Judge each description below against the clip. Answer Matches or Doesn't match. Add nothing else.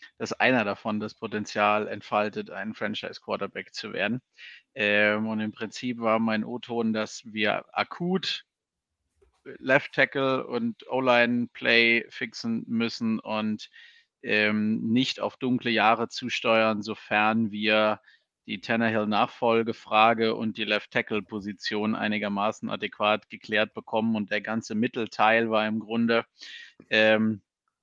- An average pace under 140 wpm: Matches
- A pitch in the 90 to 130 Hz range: Matches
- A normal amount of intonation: Doesn't match